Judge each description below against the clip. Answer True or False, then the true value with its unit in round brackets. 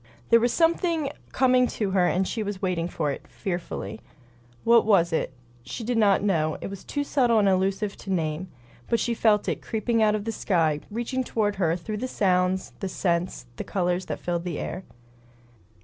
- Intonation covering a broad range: False (4.4 semitones)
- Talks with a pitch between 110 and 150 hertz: False (195 Hz)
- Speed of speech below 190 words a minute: False (195 wpm)